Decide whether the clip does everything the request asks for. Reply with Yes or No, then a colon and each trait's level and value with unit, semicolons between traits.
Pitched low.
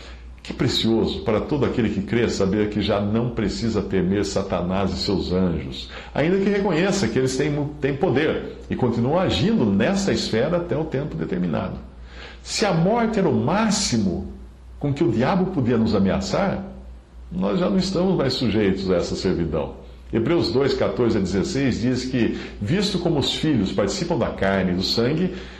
Yes: low, 115 Hz